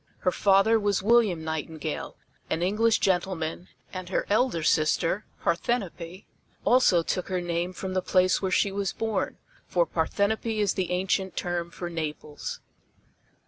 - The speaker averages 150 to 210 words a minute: No, average, 140 wpm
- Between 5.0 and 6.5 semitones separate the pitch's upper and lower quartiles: No, average, 3.0 semitones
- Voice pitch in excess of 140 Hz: Yes, medium, 185 Hz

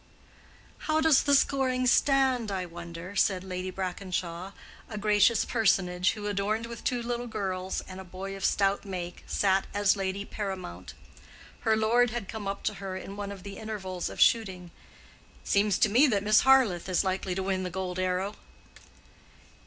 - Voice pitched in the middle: No, high, 195 Hz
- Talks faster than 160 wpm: Yes, average, 175 wpm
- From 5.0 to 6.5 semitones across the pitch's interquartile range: No, average, 2.8 semitones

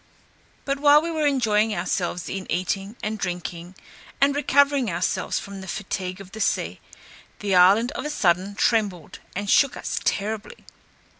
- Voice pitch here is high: Yes, high, 205 Hz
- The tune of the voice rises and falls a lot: Yes, wide, 6.3 semitones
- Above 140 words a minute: Yes, average, 155 wpm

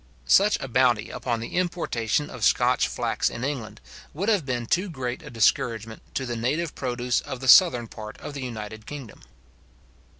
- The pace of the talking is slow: No, average, 175 wpm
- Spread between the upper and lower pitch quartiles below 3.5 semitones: No, average, 4.3 semitones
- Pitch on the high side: No, low, 125 Hz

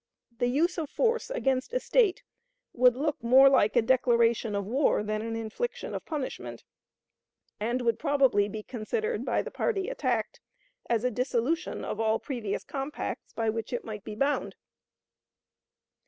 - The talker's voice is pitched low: No, very high, 250 Hz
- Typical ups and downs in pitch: Yes, average, 4.9 semitones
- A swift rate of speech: No, average, 155 wpm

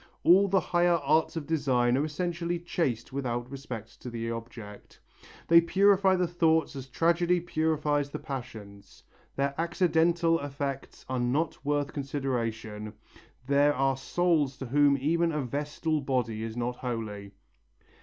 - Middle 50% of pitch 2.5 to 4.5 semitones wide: No, average, 5.2 semitones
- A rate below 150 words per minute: Yes, average, 140 wpm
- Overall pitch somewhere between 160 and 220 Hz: No, medium, 140 Hz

